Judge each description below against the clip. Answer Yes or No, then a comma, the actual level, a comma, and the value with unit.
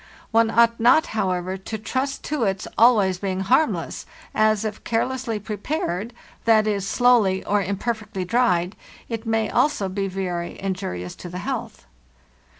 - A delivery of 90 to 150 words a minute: Yes, average, 140 wpm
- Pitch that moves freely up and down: No, average, 3.5 semitones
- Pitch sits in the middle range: No, high, 210 Hz